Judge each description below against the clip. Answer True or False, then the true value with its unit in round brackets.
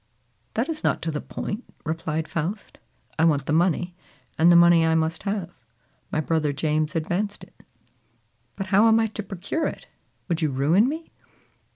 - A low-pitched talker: False (170 Hz)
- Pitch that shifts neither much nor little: True (4.3 semitones)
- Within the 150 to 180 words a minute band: True (175 wpm)